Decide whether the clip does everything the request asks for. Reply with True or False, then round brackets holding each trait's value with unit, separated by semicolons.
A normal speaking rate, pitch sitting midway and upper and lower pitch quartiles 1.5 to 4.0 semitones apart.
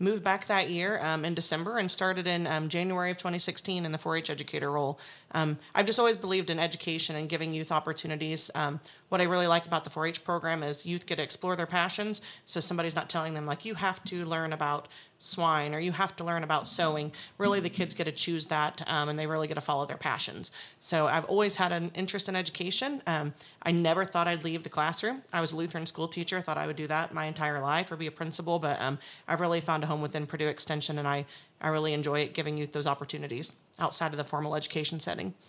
False (240 wpm; 165 Hz; 2.6 semitones)